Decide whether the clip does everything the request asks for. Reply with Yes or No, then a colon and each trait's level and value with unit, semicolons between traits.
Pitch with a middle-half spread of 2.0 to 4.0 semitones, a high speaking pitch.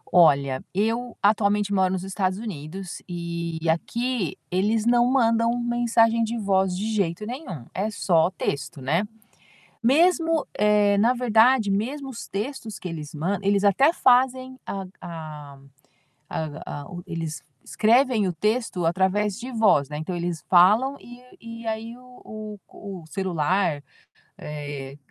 No: average, 5.2 semitones; high, 205 Hz